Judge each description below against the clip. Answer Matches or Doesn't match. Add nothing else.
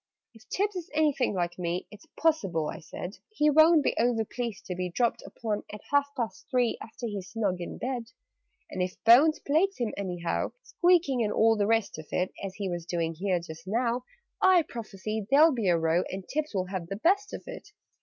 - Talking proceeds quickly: Matches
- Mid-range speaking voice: Doesn't match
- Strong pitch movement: Matches